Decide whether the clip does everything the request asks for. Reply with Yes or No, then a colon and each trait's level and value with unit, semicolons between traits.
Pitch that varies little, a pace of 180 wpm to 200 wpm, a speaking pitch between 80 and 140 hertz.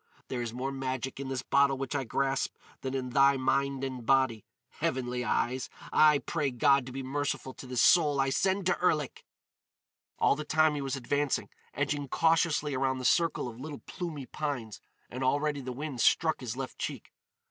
Yes: narrow, 2.2 semitones; average, 185 wpm; low, 135 Hz